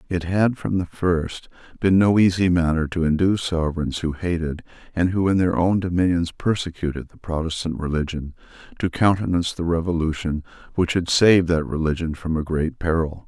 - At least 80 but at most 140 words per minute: No, average, 165 wpm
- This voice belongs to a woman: No, male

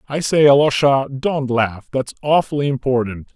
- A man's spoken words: Yes, male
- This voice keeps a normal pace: Yes, average, 145 wpm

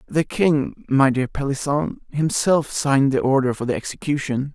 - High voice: No, medium, 140 Hz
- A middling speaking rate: Yes, average, 160 wpm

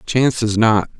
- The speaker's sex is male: Yes, male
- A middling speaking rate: Yes, average, 180 wpm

